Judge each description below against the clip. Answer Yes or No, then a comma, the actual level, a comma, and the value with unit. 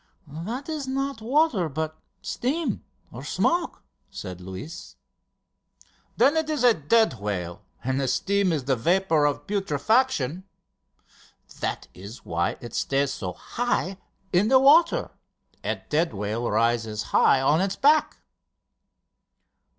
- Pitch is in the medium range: Yes, medium, 165 Hz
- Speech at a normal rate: No, slow, 125 wpm